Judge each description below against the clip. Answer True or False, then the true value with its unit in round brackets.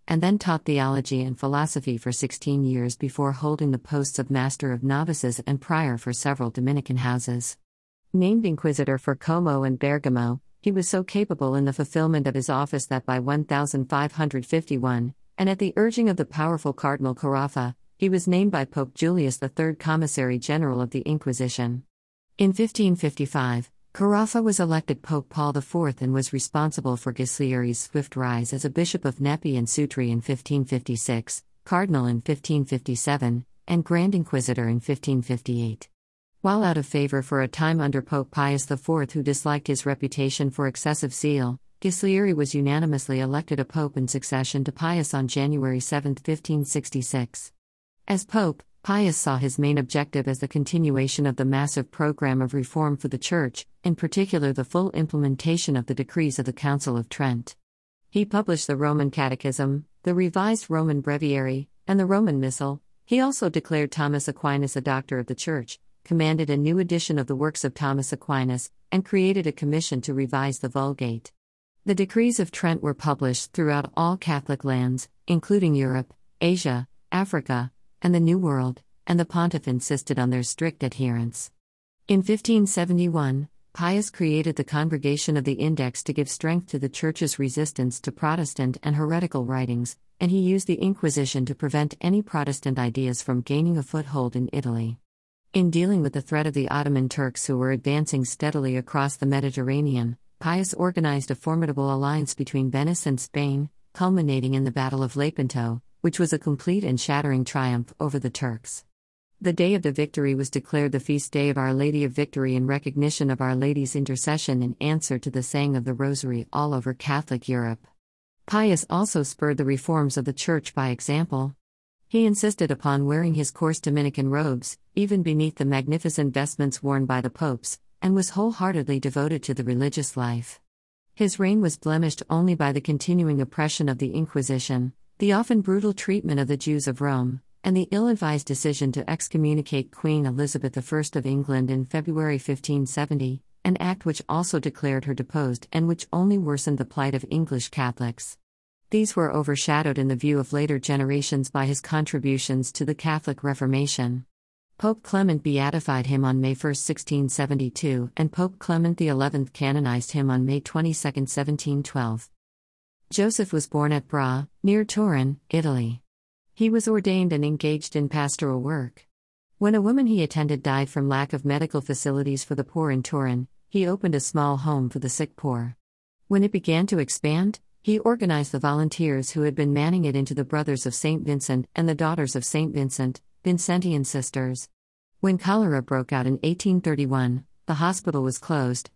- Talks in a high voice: False (145 Hz)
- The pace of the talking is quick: True (170 wpm)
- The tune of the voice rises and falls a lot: False (3.2 semitones)